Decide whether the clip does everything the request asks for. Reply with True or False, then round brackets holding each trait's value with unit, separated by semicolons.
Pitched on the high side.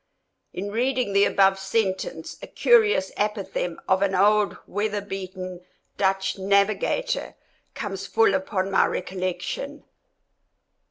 True (200 Hz)